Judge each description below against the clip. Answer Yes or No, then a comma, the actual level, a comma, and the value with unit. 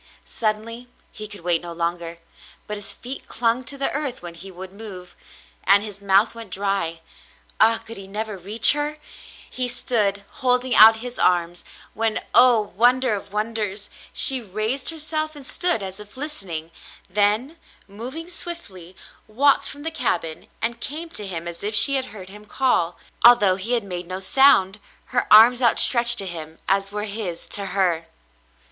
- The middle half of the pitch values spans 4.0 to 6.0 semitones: Yes, average, 4.6 semitones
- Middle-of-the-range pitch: No, high, 210 Hz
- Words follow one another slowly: No, average, 170 wpm